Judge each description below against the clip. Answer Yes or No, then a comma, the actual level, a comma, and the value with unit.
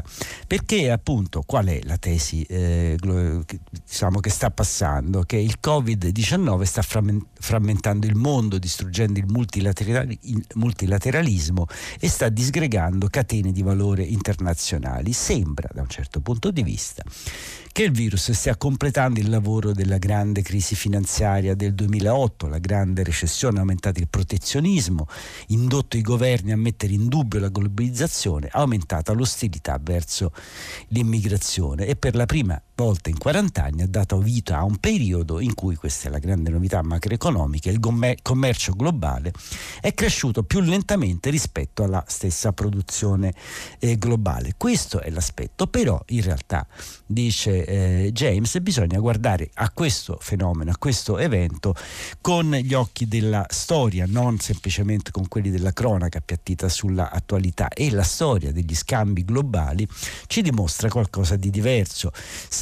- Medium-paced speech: Yes, average, 140 wpm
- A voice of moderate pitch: No, low, 100 Hz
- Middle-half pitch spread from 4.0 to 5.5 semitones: Yes, average, 4.3 semitones